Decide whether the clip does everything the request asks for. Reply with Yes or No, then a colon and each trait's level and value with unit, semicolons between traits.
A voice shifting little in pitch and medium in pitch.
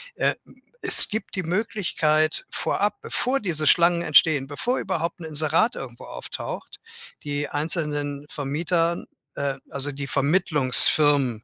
No: average, 3.3 semitones; medium, 155 Hz